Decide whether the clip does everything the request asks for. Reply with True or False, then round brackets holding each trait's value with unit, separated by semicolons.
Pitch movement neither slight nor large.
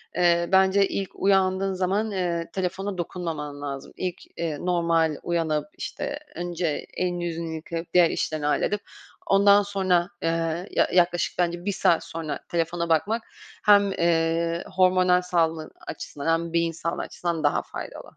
False (2.1 semitones)